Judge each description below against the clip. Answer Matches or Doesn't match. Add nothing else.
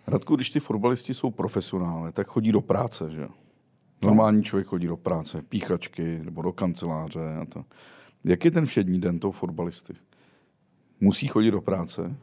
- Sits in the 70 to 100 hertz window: Matches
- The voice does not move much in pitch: Doesn't match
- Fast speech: Doesn't match